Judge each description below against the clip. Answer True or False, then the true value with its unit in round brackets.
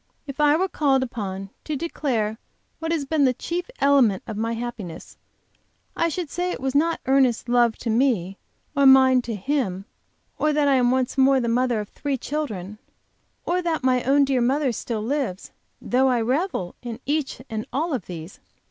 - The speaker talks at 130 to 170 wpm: False (185 wpm)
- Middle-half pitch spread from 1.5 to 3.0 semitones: False (4.2 semitones)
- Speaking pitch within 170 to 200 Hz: False (260 Hz)